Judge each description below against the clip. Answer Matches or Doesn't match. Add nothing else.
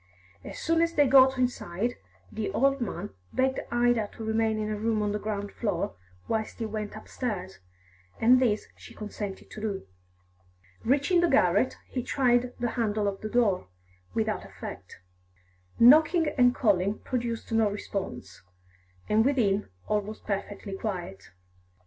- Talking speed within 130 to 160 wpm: Matches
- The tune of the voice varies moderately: Matches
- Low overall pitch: Doesn't match